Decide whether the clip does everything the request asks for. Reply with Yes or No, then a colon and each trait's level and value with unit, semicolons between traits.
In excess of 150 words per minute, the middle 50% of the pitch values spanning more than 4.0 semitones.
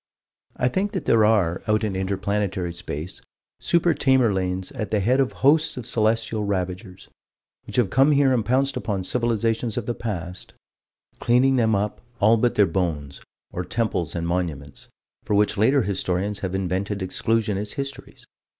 Yes: average, 160 wpm; average, 4.4 semitones